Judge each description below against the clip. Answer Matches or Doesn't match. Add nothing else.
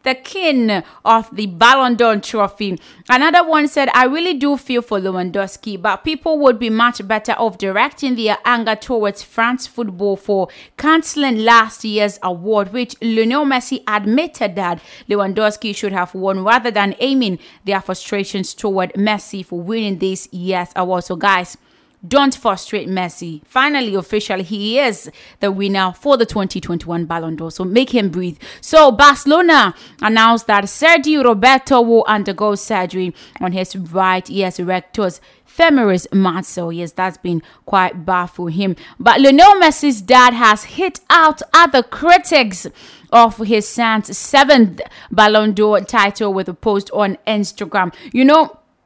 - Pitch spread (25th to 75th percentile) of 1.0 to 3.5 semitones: Doesn't match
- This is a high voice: Matches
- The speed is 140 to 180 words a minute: Matches